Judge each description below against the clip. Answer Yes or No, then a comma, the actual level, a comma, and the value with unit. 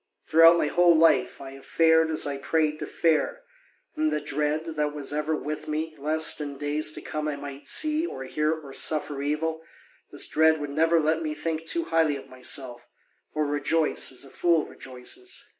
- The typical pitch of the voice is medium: Yes, medium, 155 Hz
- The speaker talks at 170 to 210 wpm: Yes, average, 190 wpm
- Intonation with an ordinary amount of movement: No, narrow, 2.1 semitones